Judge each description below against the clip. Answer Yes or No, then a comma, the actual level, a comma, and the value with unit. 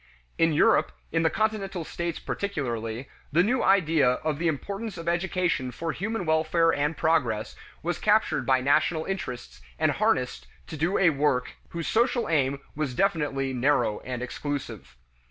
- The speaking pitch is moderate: Yes, medium, 155 Hz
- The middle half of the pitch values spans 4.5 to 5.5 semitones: Yes, average, 4.9 semitones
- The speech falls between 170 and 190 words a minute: No, average, 155 wpm